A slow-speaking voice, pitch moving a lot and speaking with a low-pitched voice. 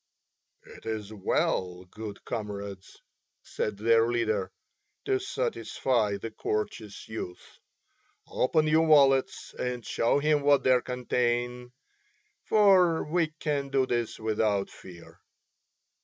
No: slow, 110 wpm; average, 5.0 semitones; low, 120 Hz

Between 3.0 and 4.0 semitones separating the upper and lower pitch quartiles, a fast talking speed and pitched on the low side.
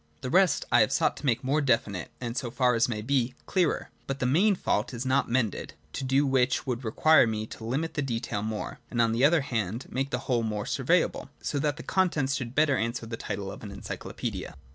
Yes: average, 3.4 semitones; fast, 230 wpm; low, 125 Hz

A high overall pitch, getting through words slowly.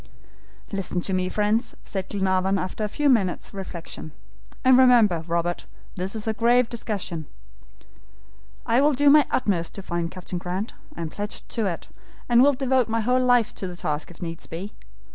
No: high, 200 Hz; average, 180 wpm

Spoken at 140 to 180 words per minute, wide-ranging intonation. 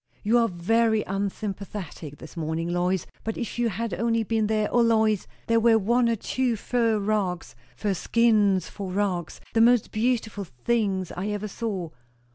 No: average, 165 wpm; average, 3.4 semitones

